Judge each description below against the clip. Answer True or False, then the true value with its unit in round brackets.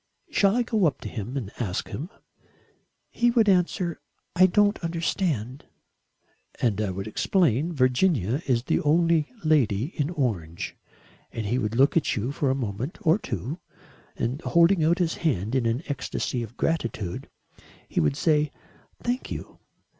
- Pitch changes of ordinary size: False (6.8 semitones)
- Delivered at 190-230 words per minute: False (155 wpm)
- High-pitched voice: False (140 Hz)